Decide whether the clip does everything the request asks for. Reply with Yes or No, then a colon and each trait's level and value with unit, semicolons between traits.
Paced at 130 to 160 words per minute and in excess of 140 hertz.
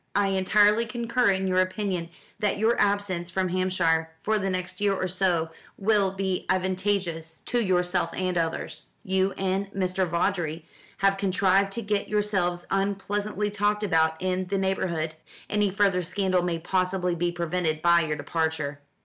Yes: average, 155 wpm; medium, 185 Hz